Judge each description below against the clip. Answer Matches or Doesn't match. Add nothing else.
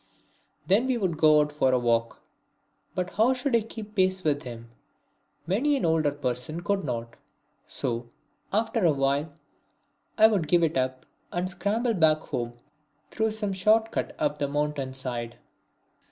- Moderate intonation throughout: Doesn't match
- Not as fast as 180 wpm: Matches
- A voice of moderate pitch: Matches